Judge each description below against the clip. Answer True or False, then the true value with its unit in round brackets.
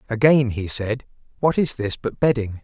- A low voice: True (120 Hz)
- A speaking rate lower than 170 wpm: False (180 wpm)